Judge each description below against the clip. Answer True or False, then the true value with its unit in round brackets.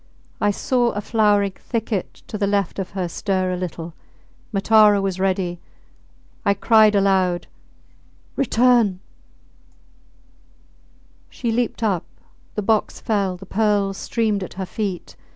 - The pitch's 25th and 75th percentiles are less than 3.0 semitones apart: True (2.5 semitones)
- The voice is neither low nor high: False (200 Hz)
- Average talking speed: False (125 wpm)